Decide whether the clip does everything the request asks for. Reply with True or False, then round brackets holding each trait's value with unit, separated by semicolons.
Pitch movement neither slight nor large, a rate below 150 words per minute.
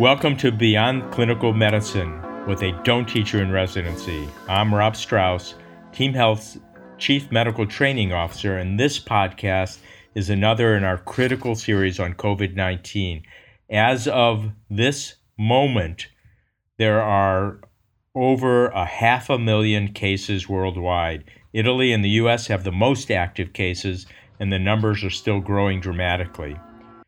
True (3.5 semitones; 135 wpm)